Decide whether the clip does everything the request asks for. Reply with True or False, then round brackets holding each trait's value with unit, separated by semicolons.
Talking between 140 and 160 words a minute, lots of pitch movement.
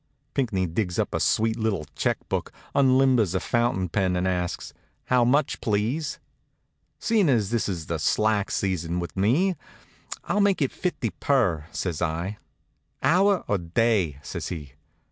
True (150 wpm; 6.5 semitones)